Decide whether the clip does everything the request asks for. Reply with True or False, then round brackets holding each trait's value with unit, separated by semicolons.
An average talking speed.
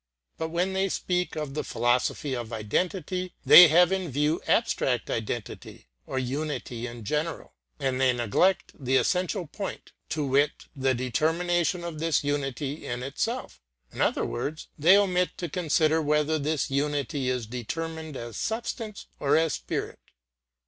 True (150 wpm)